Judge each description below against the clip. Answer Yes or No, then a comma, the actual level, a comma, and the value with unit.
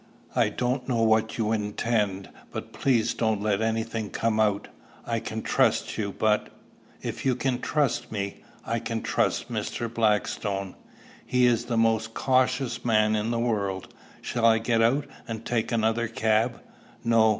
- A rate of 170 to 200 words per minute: No, average, 160 wpm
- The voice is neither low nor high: No, low, 115 Hz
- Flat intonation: Yes, narrow, 1.6 semitones